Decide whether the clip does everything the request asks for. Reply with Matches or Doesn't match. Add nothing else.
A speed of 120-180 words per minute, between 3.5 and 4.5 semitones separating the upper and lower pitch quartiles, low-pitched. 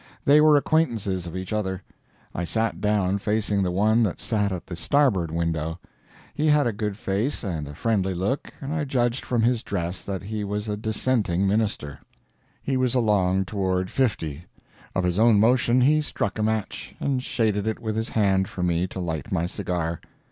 Doesn't match